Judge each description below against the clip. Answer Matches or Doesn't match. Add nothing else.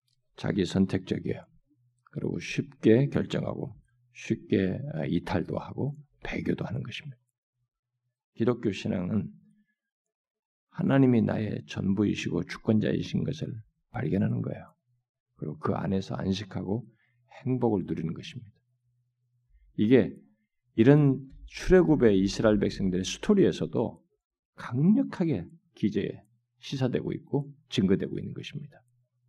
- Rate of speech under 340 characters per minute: Matches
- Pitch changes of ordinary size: Matches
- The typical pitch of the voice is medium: Doesn't match